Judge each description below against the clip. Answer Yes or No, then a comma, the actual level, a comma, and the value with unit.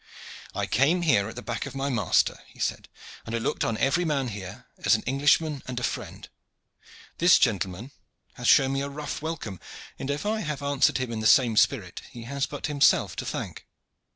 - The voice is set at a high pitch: No, low, 135 Hz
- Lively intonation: No, average, 3.9 semitones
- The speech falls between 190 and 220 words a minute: Yes, fast, 205 wpm